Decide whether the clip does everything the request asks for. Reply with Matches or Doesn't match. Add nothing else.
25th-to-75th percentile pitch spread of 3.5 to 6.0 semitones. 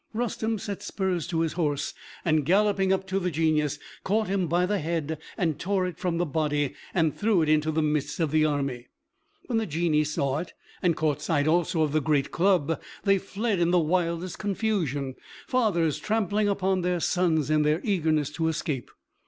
Matches